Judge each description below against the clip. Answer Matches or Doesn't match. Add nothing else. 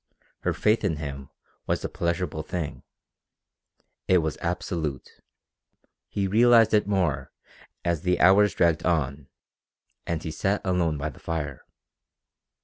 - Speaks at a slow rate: Matches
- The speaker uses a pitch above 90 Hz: Doesn't match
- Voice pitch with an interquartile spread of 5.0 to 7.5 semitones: Doesn't match